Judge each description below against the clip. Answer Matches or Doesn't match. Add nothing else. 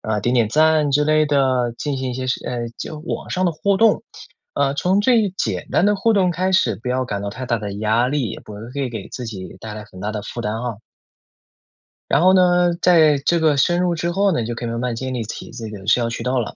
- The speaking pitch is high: Doesn't match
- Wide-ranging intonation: Matches